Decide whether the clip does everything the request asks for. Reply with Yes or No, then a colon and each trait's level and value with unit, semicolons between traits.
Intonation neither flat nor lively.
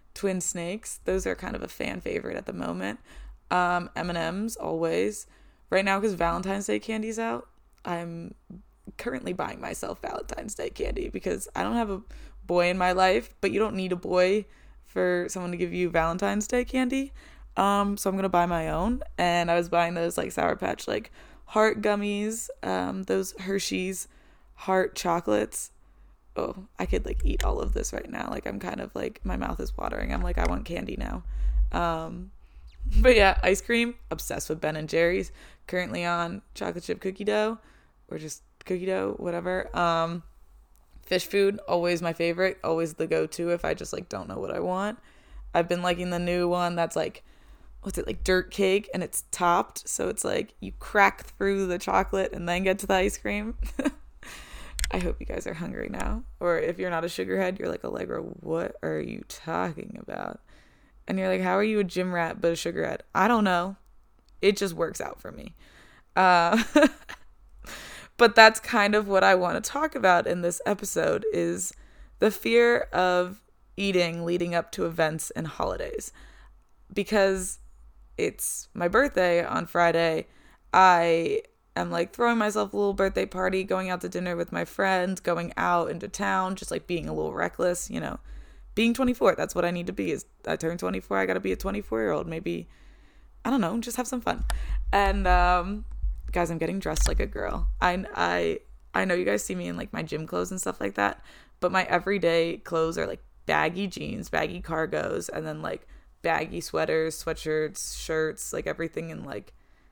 Yes: average, 3.4 semitones